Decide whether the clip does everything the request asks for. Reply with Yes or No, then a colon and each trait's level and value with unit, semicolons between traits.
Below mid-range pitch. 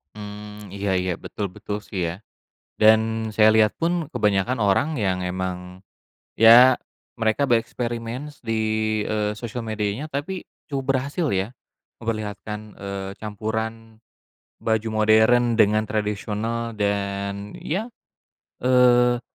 Yes: low, 110 Hz